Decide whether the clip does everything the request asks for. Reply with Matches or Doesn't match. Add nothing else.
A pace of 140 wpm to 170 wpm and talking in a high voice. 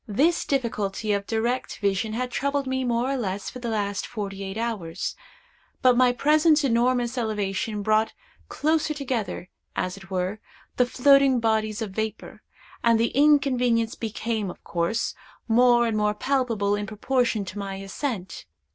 Matches